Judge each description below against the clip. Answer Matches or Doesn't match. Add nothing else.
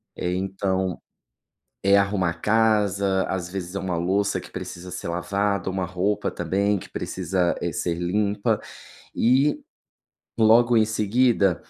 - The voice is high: Doesn't match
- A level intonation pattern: Matches